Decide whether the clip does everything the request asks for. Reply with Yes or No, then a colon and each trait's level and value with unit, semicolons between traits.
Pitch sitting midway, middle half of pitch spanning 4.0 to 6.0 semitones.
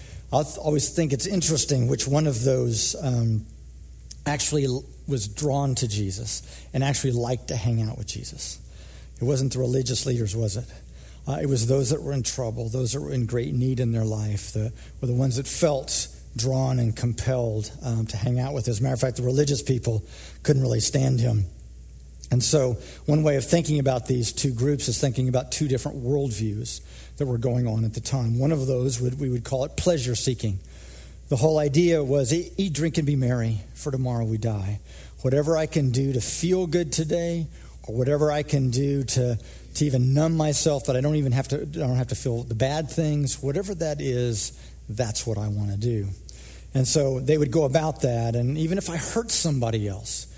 No: low, 130 Hz; average, 4.5 semitones